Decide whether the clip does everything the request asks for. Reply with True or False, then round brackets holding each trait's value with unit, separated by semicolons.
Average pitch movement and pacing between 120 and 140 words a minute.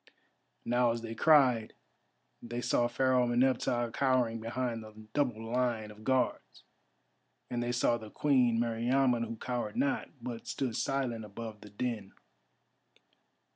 False (1.9 semitones; 135 wpm)